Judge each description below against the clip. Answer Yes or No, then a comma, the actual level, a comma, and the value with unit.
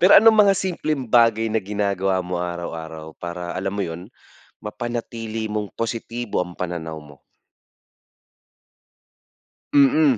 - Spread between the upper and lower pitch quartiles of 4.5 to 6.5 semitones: Yes, average, 5.3 semitones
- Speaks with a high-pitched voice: No, low, 105 Hz